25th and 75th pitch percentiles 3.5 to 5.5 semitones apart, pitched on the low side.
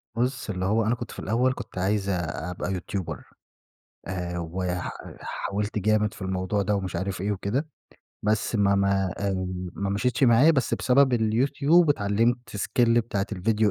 Yes: average, 3.8 semitones; low, 105 Hz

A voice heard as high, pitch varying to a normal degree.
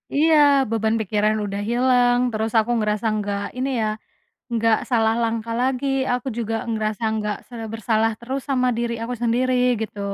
No: high, 225 Hz; narrow, 2.2 semitones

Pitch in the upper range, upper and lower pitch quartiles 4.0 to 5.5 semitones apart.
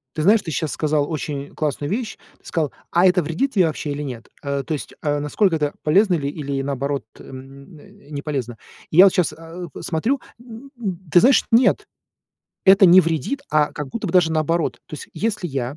No: medium, 155 Hz; average, 4.6 semitones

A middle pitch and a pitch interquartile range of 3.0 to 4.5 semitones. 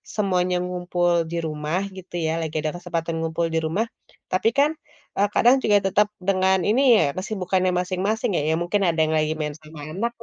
Yes: medium, 180 Hz; average, 3.5 semitones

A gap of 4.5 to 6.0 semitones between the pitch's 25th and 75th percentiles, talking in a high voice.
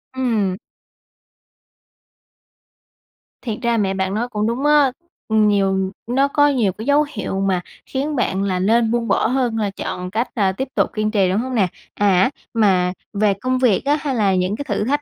Yes: average, 4.8 semitones; high, 215 Hz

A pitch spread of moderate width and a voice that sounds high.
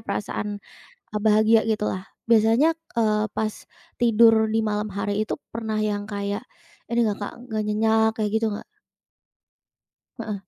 No: narrow, 1.1 semitones; high, 215 Hz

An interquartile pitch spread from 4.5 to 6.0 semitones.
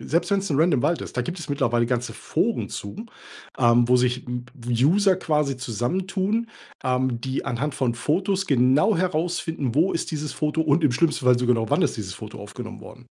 Yes: wide, 5.6 semitones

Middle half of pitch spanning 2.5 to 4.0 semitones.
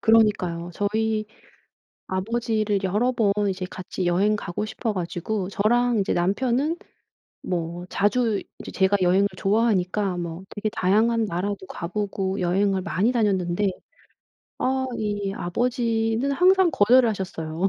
Yes: average, 3.4 semitones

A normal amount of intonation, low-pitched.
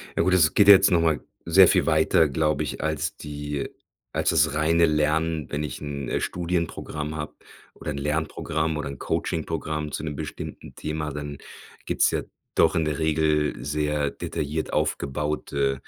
No: narrow, 1.4 semitones; very low, 75 Hz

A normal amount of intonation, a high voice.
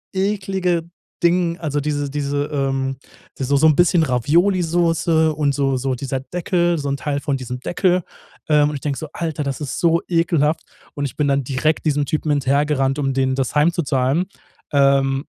No: average, 3.5 semitones; medium, 145 Hz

